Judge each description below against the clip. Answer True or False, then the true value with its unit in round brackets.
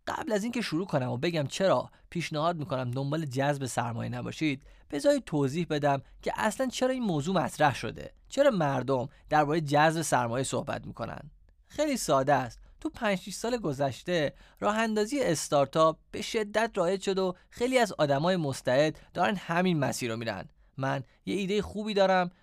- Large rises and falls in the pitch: True (6.5 semitones)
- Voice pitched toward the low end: False (160 Hz)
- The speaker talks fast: True (160 wpm)